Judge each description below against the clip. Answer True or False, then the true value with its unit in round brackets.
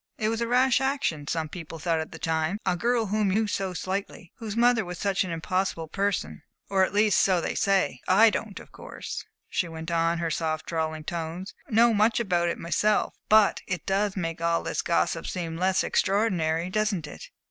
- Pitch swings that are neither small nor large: True (4.3 semitones)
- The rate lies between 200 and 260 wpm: True (205 wpm)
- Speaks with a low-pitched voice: False (185 Hz)